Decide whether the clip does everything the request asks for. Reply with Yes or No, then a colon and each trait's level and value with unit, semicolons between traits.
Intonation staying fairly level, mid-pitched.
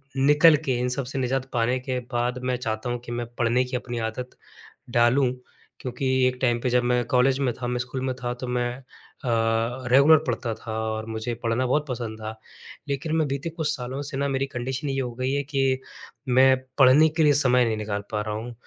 No: narrow, 1.9 semitones; low, 125 Hz